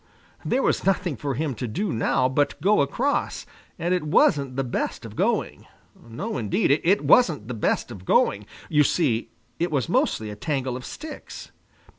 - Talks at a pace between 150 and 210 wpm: Yes, average, 175 wpm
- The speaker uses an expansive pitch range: Yes, wide, 6.2 semitones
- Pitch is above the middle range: No, medium, 140 Hz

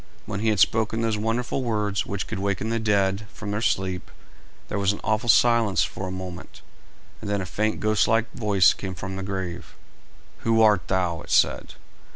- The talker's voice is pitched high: No, low, 105 Hz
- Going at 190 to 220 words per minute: Yes, average, 195 wpm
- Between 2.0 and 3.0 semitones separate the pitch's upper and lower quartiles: Yes, average, 2.7 semitones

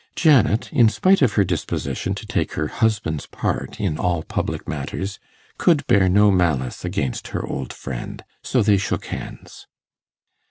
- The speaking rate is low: No, average, 155 wpm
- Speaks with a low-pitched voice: Yes, low, 100 Hz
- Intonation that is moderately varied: No, wide, 6.3 semitones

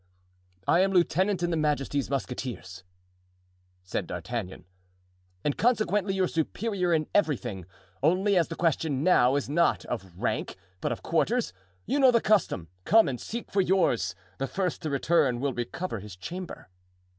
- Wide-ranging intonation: Yes, wide, 7.7 semitones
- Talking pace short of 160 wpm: Yes, average, 145 wpm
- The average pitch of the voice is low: No, medium, 155 Hz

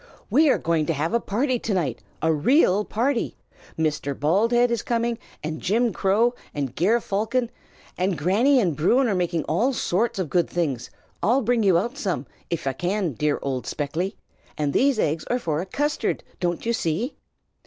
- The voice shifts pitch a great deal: Yes, wide, 6.9 semitones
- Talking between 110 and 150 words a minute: No, average, 185 wpm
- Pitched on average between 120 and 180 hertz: No, high, 190 Hz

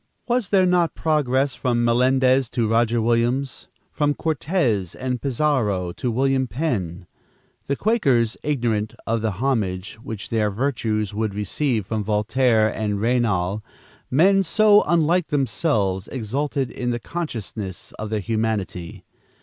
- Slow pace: Yes, slow, 130 wpm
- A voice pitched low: Yes, low, 120 Hz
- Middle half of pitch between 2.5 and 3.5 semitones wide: No, average, 4.7 semitones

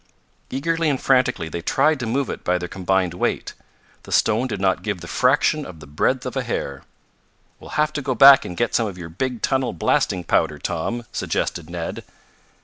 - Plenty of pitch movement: Yes, wide, 7.2 semitones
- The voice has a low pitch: Yes, low, 110 Hz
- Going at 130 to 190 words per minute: No, average, 200 wpm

